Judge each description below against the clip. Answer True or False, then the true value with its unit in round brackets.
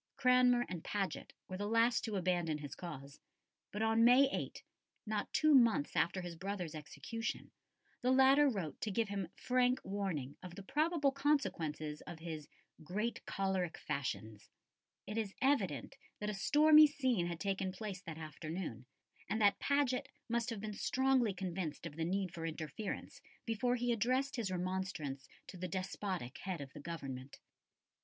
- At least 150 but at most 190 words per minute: True (160 wpm)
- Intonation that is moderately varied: False (6.4 semitones)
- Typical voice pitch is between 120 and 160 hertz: False (195 Hz)